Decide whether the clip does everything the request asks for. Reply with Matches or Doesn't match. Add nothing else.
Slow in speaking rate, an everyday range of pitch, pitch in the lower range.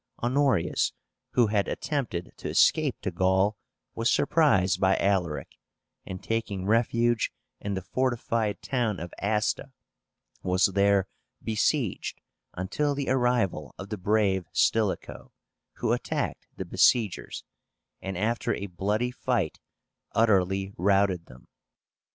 Matches